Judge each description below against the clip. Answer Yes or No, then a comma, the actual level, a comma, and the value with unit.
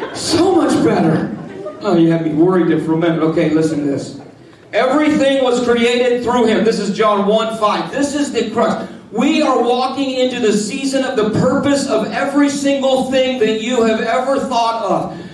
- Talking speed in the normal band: Yes, average, 190 wpm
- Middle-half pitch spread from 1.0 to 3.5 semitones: No, average, 4.4 semitones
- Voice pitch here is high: Yes, high, 235 Hz